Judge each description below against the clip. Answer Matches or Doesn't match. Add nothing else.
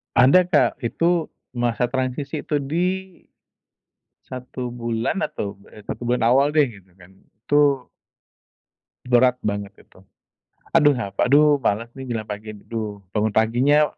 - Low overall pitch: Matches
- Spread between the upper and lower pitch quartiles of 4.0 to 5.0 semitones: Matches